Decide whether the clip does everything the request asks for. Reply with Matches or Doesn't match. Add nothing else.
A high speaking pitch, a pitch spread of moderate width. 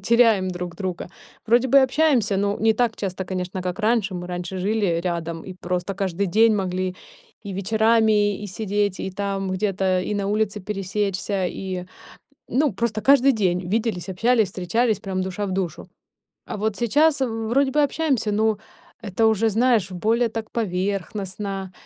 Matches